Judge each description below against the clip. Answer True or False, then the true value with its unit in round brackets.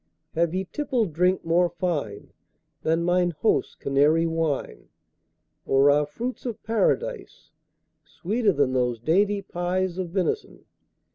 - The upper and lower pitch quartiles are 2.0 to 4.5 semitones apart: True (4.2 semitones)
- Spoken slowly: True (125 wpm)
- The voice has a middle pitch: True (175 Hz)